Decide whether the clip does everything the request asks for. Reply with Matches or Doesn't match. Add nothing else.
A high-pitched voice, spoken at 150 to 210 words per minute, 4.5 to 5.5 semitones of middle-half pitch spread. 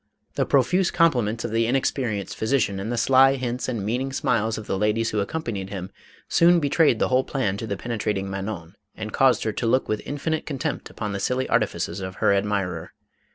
Doesn't match